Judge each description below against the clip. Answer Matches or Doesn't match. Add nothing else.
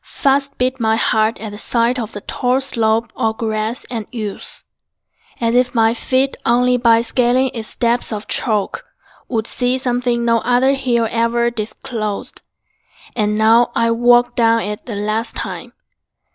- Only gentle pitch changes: Matches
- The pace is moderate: Matches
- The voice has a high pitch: Matches